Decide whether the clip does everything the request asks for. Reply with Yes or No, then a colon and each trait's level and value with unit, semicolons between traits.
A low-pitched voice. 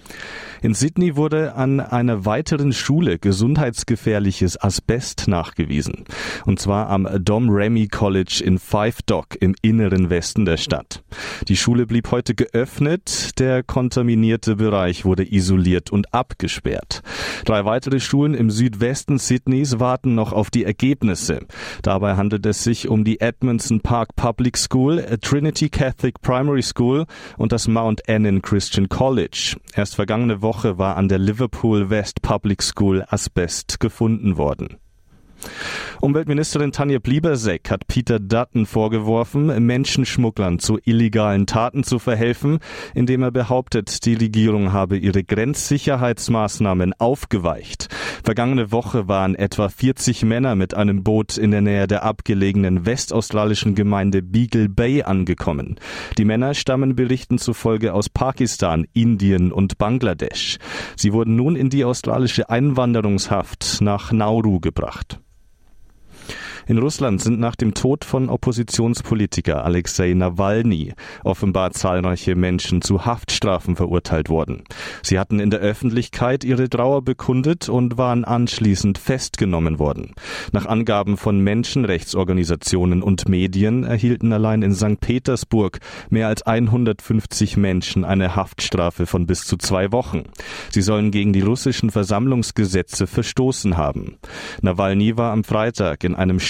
Yes: low, 110 Hz